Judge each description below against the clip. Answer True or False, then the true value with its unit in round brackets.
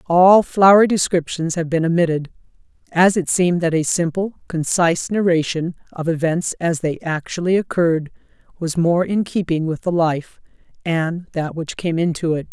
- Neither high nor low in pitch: True (170 Hz)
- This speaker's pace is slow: False (160 wpm)